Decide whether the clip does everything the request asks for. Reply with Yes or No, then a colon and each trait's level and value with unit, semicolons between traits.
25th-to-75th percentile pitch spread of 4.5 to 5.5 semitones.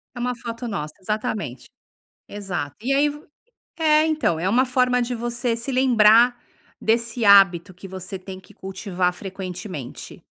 Yes: average, 4.8 semitones